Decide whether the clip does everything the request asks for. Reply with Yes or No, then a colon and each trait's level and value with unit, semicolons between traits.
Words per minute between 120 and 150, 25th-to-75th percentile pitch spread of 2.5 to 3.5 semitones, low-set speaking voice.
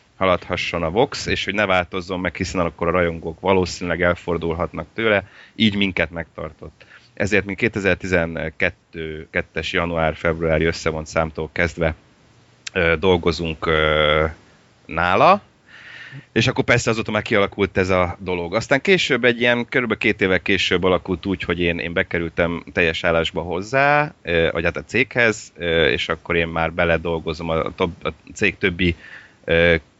Yes: average, 130 wpm; average, 2.9 semitones; very low, 90 Hz